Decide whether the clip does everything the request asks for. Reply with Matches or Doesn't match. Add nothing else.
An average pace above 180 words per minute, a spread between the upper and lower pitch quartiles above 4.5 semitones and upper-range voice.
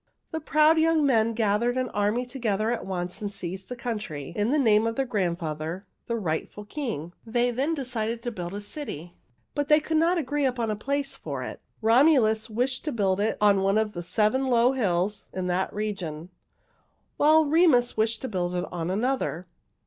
Matches